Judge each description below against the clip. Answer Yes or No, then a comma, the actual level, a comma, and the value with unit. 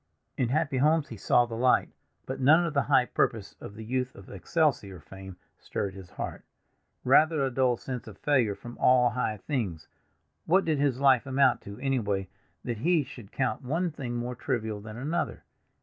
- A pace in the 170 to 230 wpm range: Yes, average, 180 wpm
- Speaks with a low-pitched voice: Yes, low, 125 Hz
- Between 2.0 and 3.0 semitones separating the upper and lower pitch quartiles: No, average, 4.3 semitones